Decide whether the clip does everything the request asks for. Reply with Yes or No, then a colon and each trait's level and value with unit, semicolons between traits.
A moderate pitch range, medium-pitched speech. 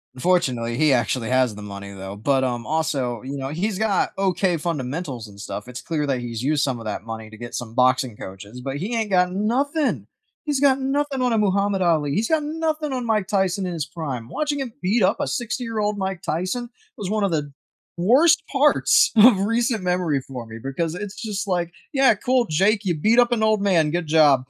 No: wide, 8.9 semitones; medium, 180 Hz